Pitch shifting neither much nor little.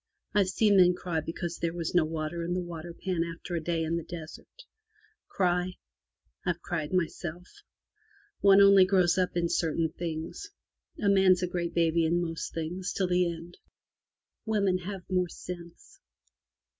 No: narrow, 1.7 semitones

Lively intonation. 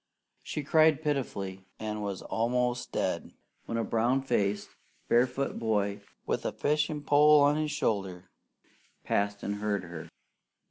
Yes: wide, 6.1 semitones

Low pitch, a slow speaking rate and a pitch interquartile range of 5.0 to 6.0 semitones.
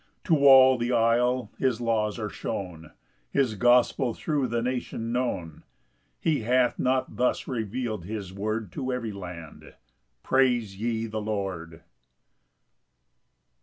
No: low, 115 Hz; slow, 130 wpm; average, 3.4 semitones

